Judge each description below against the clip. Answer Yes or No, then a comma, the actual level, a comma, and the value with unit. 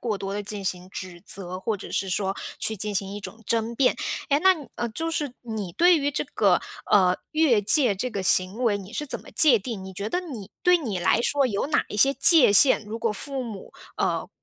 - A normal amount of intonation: No, wide, 5.9 semitones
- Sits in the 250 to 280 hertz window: No, high, 220 Hz